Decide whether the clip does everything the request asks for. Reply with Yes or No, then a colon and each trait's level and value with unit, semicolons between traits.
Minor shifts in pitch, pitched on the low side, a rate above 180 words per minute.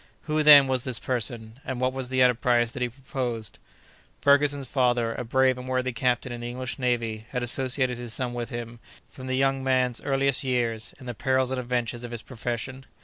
Yes: narrow, 1.7 semitones; low, 125 Hz; fast, 205 wpm